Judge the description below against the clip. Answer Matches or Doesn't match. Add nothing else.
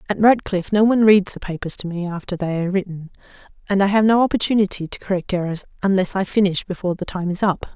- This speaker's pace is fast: Matches